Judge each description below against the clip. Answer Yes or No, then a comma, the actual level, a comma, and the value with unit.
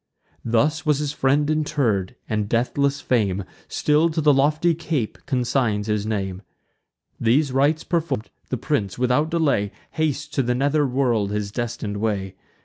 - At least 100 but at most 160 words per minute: Yes, average, 145 wpm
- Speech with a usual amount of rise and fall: No, wide, 5.7 semitones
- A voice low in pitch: Yes, low, 130 Hz